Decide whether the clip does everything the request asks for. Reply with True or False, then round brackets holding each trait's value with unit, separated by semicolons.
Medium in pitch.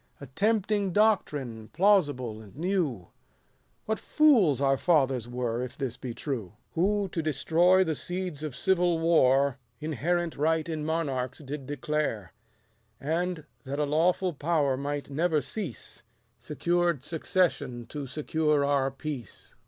True (150 Hz)